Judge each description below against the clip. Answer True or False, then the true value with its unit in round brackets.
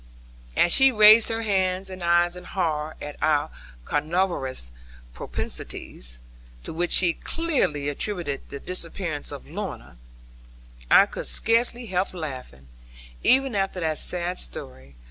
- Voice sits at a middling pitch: True (175 Hz)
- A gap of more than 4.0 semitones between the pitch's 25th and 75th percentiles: True (5.0 semitones)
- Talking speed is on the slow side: True (125 wpm)